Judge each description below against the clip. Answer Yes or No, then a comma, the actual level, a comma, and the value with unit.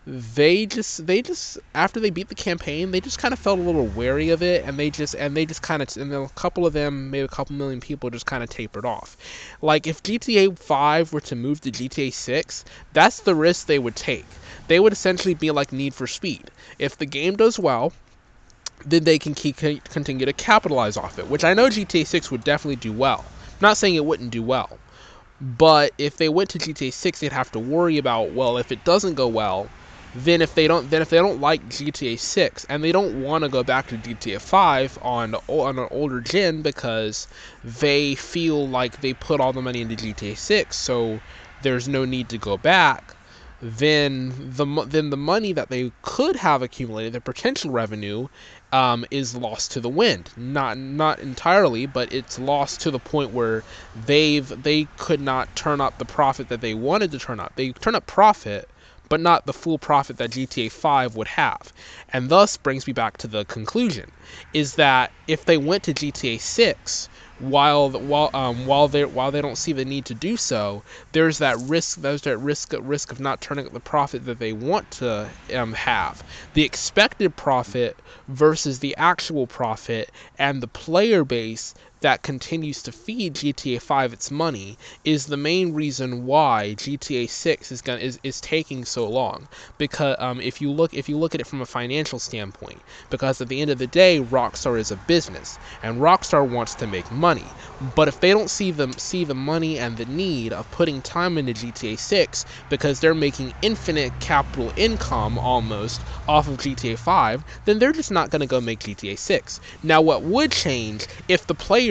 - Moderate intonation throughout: Yes, average, 4.3 semitones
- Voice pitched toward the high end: No, medium, 140 Hz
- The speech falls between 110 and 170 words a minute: No, average, 200 wpm